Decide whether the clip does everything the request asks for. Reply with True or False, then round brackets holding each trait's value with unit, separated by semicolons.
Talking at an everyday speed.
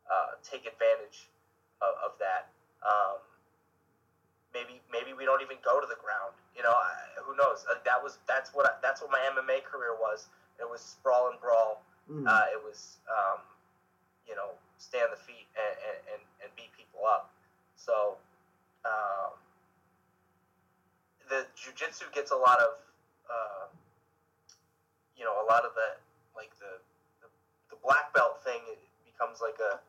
True (160 wpm)